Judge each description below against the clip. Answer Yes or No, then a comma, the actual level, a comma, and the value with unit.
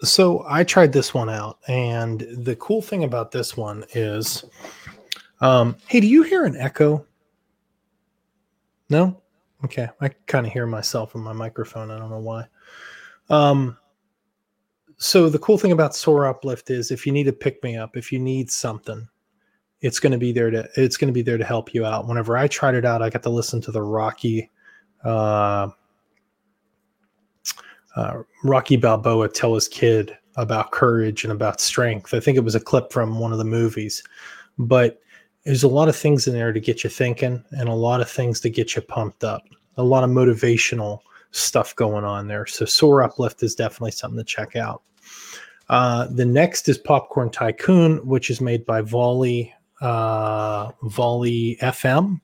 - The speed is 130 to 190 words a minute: Yes, average, 180 wpm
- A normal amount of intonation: Yes, average, 3.4 semitones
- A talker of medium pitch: No, low, 120 Hz